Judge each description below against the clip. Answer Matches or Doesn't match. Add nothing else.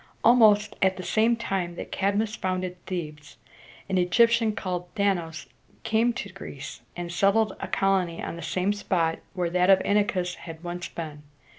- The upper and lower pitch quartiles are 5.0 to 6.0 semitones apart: Doesn't match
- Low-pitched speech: Doesn't match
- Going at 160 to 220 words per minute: Matches